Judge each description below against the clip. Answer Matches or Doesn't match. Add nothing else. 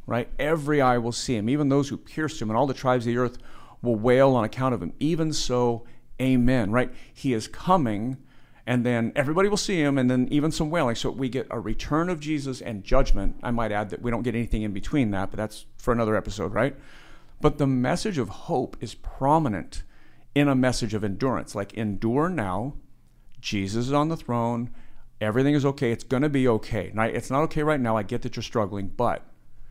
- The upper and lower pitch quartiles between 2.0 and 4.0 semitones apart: Matches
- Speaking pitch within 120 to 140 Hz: Matches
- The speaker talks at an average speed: Doesn't match